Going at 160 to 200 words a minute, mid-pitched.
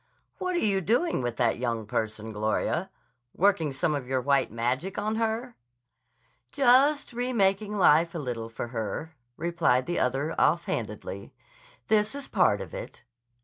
No: average, 145 wpm; medium, 165 Hz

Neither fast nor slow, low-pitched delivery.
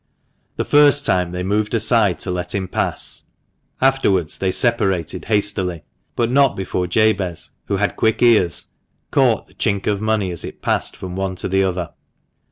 Yes: average, 170 wpm; very low, 95 Hz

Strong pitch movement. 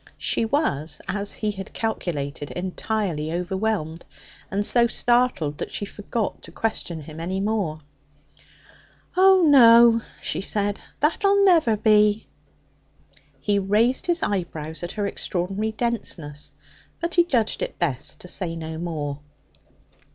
Yes: wide, 5.7 semitones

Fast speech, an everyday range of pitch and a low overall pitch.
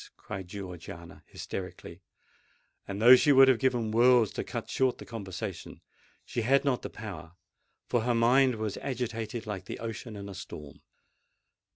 No: average, 155 wpm; average, 4.3 semitones; low, 110 Hz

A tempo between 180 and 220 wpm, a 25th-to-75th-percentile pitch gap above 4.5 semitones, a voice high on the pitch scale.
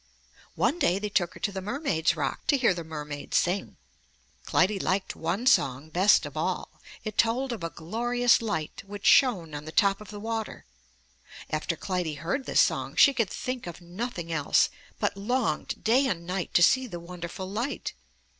Yes: average, 185 wpm; wide, 5.6 semitones; high, 195 Hz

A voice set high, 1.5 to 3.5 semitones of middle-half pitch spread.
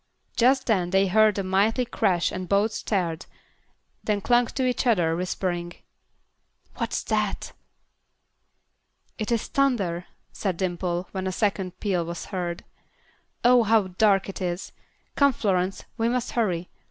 No: high, 195 Hz; average, 4.0 semitones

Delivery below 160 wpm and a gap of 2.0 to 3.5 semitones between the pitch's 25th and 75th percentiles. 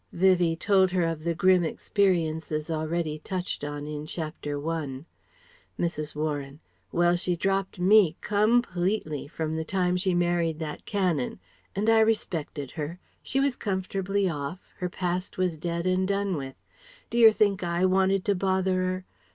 Yes: average, 150 wpm; average, 3.2 semitones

